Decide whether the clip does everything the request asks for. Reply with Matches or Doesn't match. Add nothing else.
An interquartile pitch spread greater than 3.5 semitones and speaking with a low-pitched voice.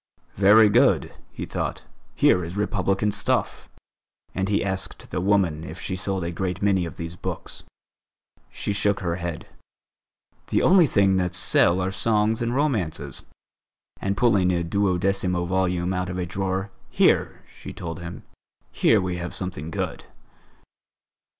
Doesn't match